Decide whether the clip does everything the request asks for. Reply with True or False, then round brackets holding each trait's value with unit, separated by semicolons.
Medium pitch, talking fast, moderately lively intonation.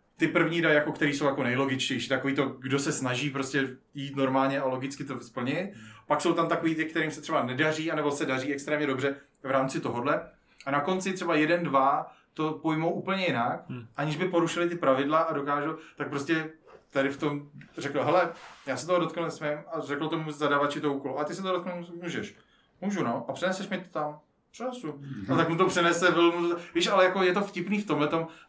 True (155 Hz; 210 wpm; 3.5 semitones)